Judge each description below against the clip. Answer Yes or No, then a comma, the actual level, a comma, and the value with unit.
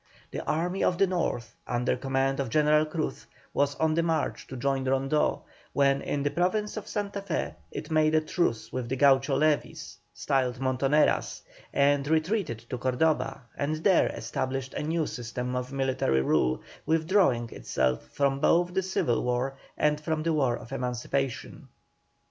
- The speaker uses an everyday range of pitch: Yes, average, 3.7 semitones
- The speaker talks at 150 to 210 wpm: Yes, average, 160 wpm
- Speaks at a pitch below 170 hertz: Yes, medium, 140 Hz